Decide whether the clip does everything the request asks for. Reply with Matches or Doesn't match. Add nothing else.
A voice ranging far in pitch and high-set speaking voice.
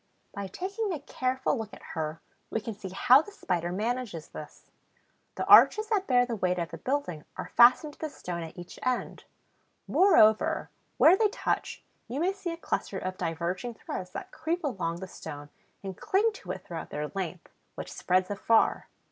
Matches